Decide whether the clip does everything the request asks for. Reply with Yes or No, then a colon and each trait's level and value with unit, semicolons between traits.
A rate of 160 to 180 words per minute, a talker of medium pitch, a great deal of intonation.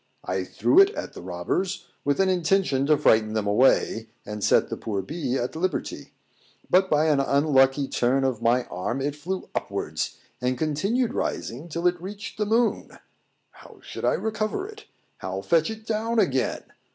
Yes: average, 175 wpm; medium, 150 Hz; wide, 7.2 semitones